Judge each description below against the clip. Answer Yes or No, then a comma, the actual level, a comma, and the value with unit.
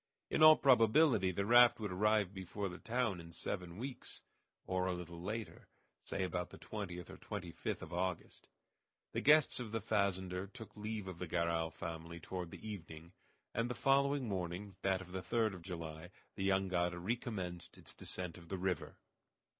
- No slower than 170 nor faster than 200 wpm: Yes, average, 180 wpm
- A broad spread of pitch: No, average, 3.7 semitones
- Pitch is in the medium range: No, very low, 95 Hz